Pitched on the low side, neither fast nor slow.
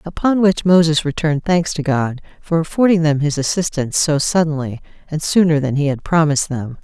No: medium, 155 Hz; average, 185 wpm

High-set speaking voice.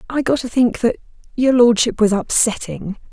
Yes: high, 235 Hz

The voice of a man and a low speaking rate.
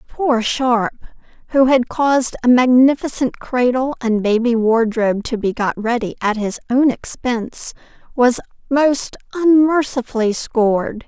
No: female; slow, 125 wpm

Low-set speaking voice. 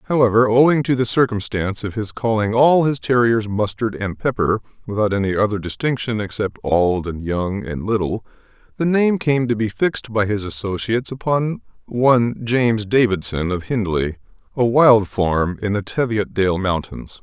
Yes: low, 110 Hz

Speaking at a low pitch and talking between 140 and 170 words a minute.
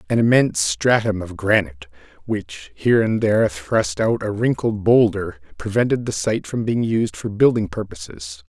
Yes: low, 110 Hz; average, 160 wpm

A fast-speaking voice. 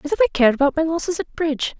Yes: fast, 300 wpm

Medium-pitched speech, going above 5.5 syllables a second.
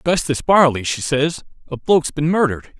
No: medium, 150 Hz; 5.4 syllables/s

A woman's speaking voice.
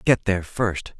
No: male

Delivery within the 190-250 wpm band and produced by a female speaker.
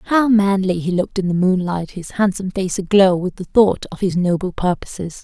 Yes: fast, 205 wpm; female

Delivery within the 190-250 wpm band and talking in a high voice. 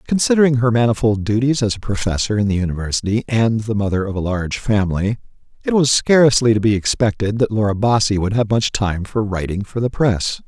No: average, 200 wpm; low, 110 Hz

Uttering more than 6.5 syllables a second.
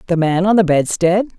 No: 5.5 syllables/s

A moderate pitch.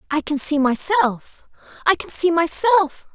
No: very high, 325 Hz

